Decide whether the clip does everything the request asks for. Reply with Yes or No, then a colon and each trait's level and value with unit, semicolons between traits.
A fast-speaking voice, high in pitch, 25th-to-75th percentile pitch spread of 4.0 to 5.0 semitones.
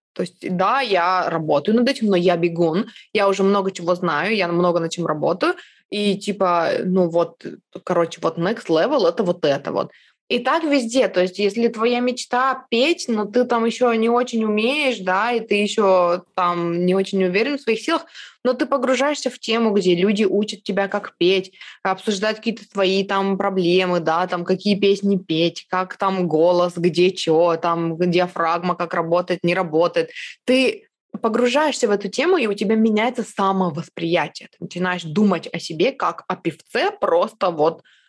Yes: fast, 175 wpm; high, 195 Hz; average, 4.6 semitones